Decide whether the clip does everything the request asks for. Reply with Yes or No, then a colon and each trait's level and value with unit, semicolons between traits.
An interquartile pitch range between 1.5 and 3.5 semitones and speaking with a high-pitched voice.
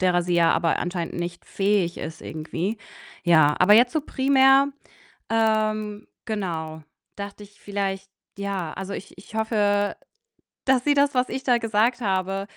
No: average, 4.1 semitones; high, 200 Hz